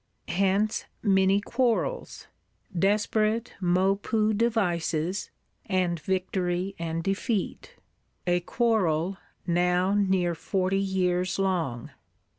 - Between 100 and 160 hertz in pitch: No, high, 190 Hz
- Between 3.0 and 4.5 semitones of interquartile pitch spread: No, narrow, 2.6 semitones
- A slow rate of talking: Yes, slow, 80 wpm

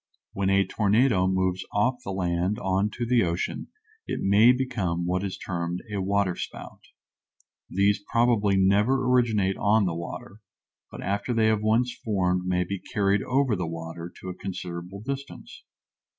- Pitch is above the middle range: No, low, 100 Hz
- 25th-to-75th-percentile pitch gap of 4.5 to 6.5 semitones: No, average, 3.4 semitones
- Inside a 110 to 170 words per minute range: Yes, average, 155 wpm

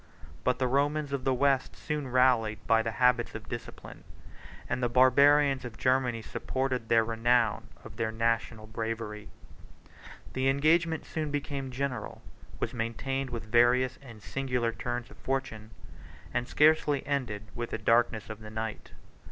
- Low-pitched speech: Yes, low, 125 Hz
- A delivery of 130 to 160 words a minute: Yes, average, 150 wpm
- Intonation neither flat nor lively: Yes, average, 3.1 semitones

